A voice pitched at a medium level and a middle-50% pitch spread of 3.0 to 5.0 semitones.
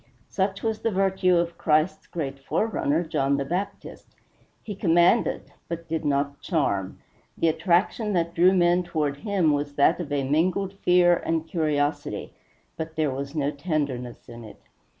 Yes: medium, 165 Hz; average, 3.9 semitones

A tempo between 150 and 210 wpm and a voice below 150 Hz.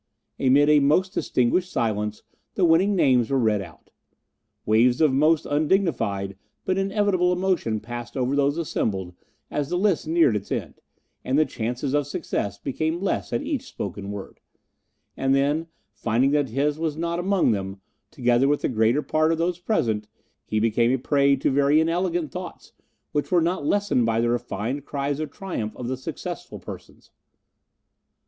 Yes: average, 165 wpm; medium, 140 Hz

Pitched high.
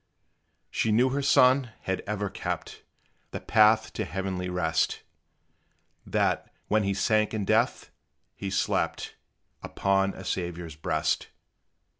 No: low, 100 Hz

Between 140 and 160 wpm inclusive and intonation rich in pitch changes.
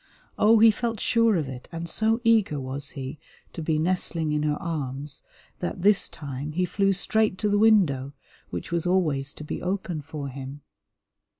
No: average, 180 wpm; wide, 6.0 semitones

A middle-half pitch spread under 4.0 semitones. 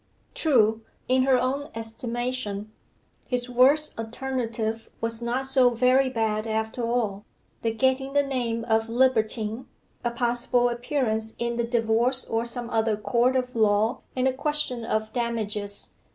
Yes: narrow, 2.4 semitones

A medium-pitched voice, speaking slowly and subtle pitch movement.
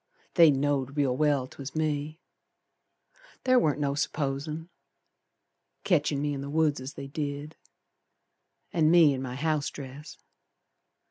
Yes: medium, 145 Hz; slow, 130 wpm; narrow, 2.0 semitones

